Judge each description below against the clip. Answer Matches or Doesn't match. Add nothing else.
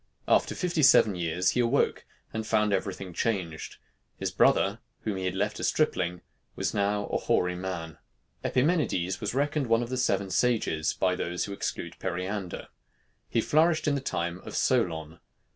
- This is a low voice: Matches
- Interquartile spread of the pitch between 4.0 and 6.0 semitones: Matches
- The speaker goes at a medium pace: Matches